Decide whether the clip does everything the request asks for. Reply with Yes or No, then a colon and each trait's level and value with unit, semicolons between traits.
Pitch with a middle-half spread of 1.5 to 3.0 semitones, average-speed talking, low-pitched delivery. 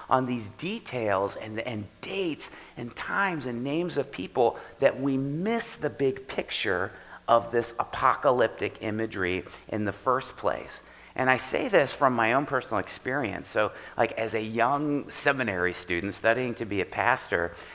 No: average, 4.1 semitones; average, 160 wpm; low, 125 Hz